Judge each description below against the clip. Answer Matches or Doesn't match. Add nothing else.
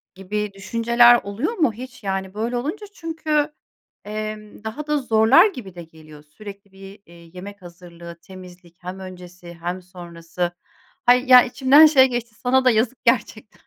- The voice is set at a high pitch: Matches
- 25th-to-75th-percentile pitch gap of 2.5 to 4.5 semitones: Doesn't match